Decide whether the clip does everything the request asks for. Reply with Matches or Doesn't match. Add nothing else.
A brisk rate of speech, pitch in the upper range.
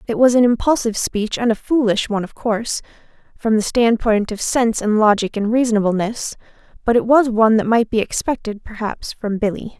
Doesn't match